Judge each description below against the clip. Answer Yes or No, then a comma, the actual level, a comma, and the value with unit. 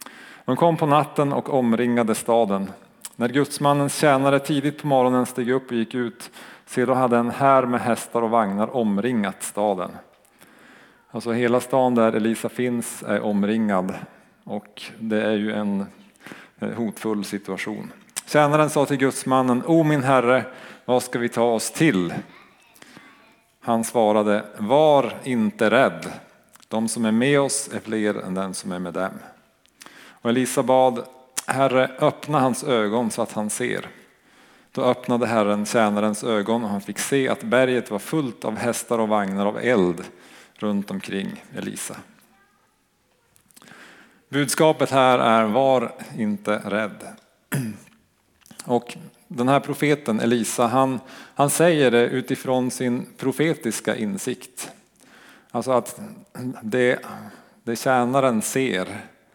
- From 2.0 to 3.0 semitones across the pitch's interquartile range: No, average, 3.4 semitones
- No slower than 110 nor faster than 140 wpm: Yes, average, 135 wpm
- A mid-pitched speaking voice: No, low, 125 Hz